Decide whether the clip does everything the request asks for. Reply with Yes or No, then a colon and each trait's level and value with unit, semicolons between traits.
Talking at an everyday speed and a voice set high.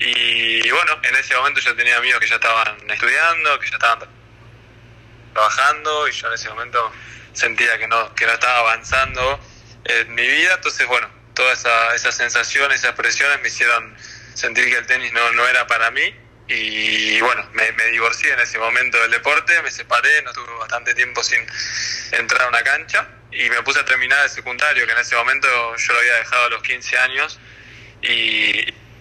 No: average, 190 wpm; low, 115 Hz